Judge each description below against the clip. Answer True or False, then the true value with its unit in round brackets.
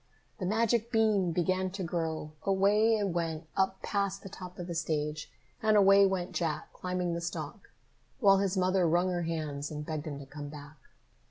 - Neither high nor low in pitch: True (180 Hz)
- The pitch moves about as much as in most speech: True (3.6 semitones)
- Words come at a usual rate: True (185 wpm)